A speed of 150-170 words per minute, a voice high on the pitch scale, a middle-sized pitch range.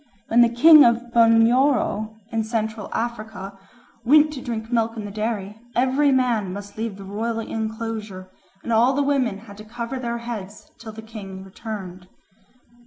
No: average, 165 wpm; high, 225 Hz; narrow, 2.1 semitones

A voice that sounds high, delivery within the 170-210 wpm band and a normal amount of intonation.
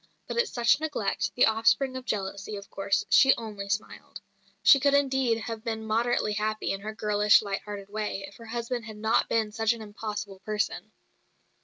No: high, 215 Hz; average, 185 wpm; narrow, 2.2 semitones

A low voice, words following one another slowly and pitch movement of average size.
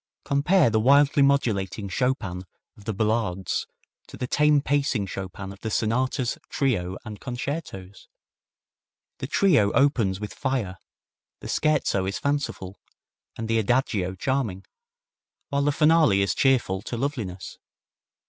No: low, 115 Hz; slow, 130 wpm; wide, 6.3 semitones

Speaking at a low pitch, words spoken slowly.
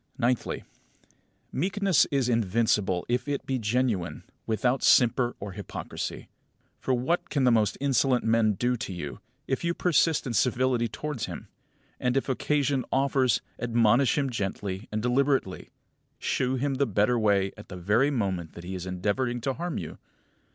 No: low, 120 Hz; average, 160 wpm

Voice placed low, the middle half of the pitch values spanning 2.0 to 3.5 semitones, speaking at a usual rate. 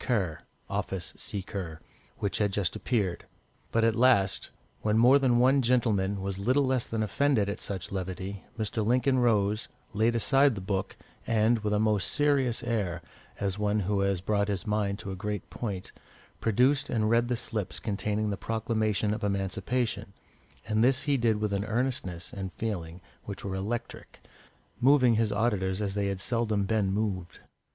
Yes: low, 105 Hz; average, 3.2 semitones; average, 170 wpm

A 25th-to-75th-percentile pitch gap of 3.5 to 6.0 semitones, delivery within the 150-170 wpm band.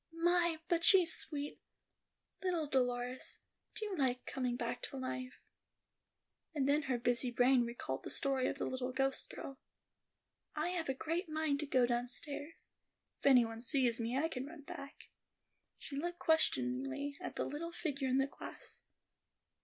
Yes: average, 4.1 semitones; average, 160 wpm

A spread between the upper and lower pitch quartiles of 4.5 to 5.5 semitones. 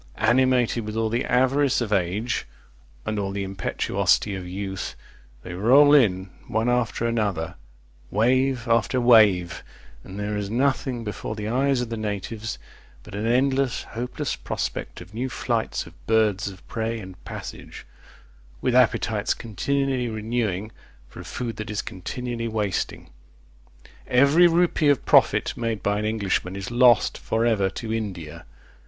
No: average, 3.4 semitones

